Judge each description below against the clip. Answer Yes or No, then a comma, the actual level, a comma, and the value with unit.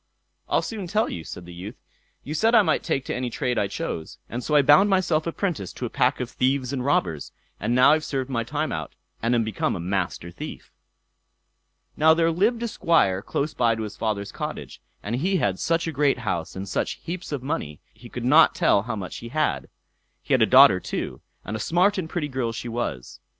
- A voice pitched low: Yes, low, 125 Hz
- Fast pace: Yes, fast, 225 wpm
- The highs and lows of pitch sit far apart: Yes, wide, 7.4 semitones